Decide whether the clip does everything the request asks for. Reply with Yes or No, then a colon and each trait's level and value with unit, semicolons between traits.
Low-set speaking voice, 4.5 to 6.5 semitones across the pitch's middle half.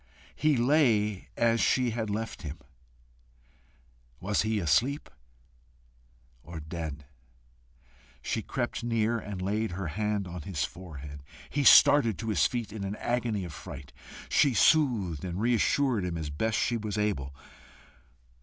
Yes: low, 105 Hz; wide, 5.4 semitones